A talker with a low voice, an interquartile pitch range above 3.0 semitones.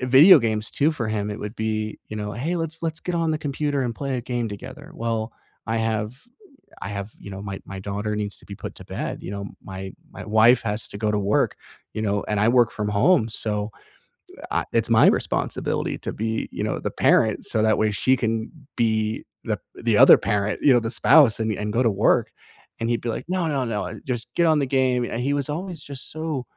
Yes: low, 115 Hz; average, 4.3 semitones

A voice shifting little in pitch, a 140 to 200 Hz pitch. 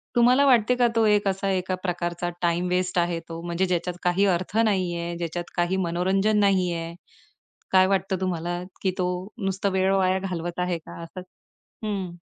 Yes: narrow, 2.0 semitones; medium, 185 Hz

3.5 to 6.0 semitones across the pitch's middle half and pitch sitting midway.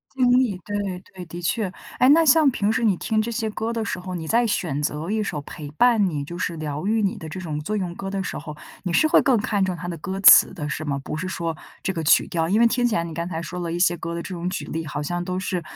Yes: average, 4.5 semitones; medium, 180 Hz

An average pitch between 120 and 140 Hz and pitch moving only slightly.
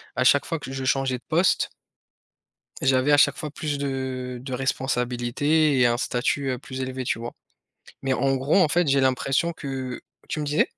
Yes: low, 135 Hz; narrow, 2.2 semitones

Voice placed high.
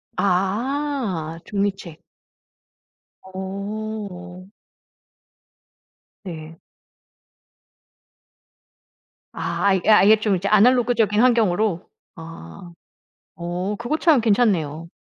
Yes: high, 200 Hz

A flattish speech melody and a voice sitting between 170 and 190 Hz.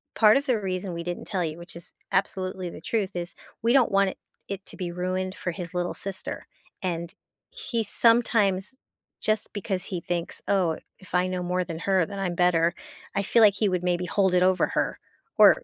Yes: narrow, 2.2 semitones; medium, 185 Hz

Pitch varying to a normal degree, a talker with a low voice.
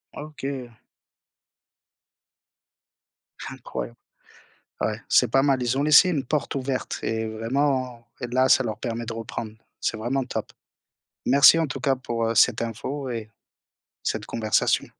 Yes: average, 3.1 semitones; low, 125 Hz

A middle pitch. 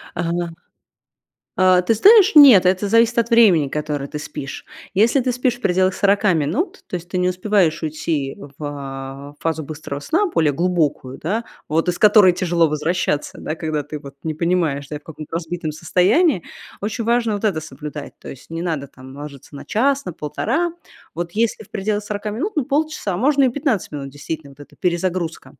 Yes: medium, 175 Hz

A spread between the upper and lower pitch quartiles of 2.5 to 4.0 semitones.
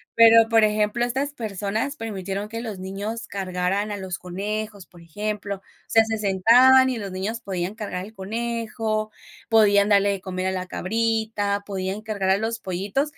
Yes: average, 2.8 semitones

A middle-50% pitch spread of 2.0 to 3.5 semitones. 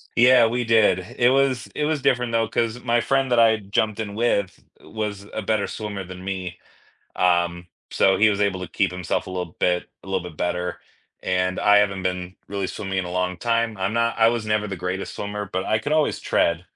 No: average, 3.9 semitones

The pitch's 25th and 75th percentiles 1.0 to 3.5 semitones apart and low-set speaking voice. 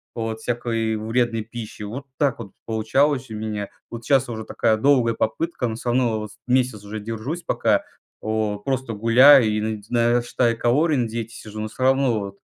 Yes: narrow, 2.6 semitones; low, 115 Hz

